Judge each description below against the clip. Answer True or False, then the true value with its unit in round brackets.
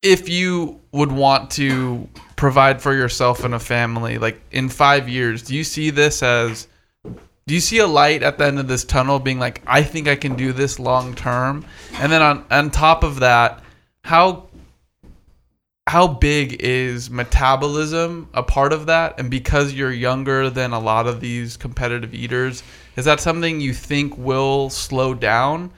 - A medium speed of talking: True (175 wpm)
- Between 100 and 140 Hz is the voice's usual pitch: True (135 Hz)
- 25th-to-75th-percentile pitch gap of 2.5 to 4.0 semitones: True (3.0 semitones)